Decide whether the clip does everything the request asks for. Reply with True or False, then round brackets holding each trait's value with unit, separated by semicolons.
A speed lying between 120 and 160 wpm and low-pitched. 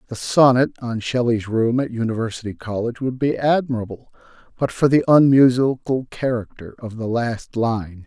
True (150 wpm; 120 Hz)